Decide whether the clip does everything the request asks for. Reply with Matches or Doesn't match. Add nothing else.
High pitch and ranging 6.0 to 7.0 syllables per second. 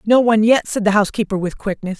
Matches